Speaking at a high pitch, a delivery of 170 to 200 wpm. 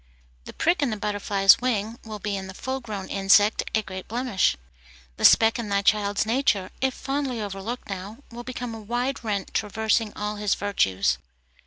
Yes: high, 210 Hz; average, 180 wpm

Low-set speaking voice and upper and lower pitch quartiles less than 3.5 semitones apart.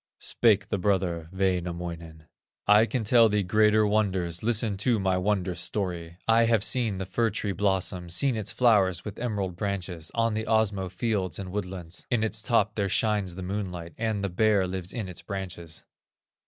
Yes: low, 100 Hz; average, 3.1 semitones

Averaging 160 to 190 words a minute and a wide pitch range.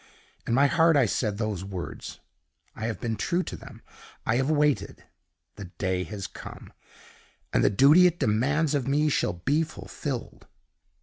Yes: average, 165 wpm; wide, 6.0 semitones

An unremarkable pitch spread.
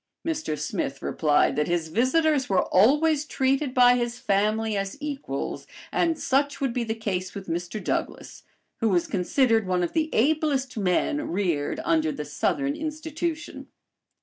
No: wide, 8.3 semitones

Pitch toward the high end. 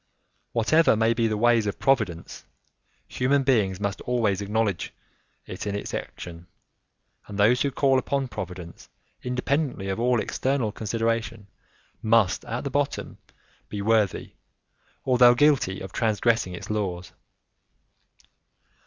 No: low, 115 Hz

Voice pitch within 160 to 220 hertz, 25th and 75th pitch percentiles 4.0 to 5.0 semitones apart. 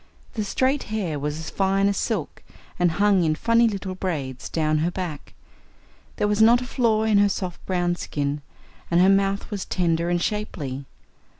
Yes: medium, 185 Hz; average, 4.4 semitones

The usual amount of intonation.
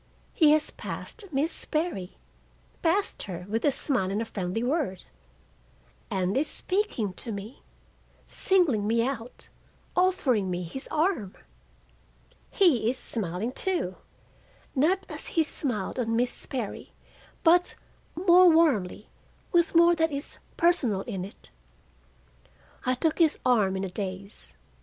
No: wide, 9.0 semitones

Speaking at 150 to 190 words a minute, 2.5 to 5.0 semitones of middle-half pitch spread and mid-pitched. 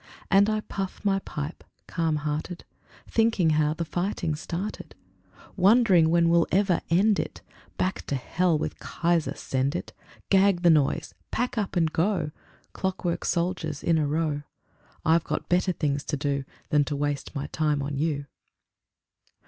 Yes: average, 155 wpm; average, 3.7 semitones; medium, 165 Hz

